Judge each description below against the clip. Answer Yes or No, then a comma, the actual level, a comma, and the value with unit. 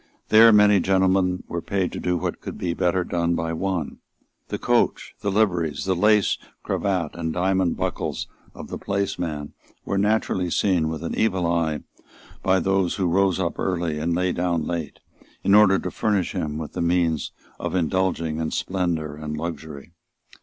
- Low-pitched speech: Yes, very low, 90 Hz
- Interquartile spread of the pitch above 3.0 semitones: No, average, 2.7 semitones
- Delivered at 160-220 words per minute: Yes, average, 170 wpm